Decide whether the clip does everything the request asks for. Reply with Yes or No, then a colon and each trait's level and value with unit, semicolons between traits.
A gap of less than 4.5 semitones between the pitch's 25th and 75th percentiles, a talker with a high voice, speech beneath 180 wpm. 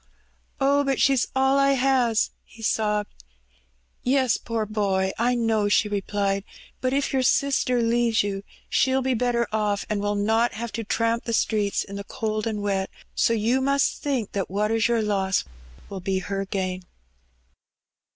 Yes: average, 3.5 semitones; high, 225 Hz; average, 170 wpm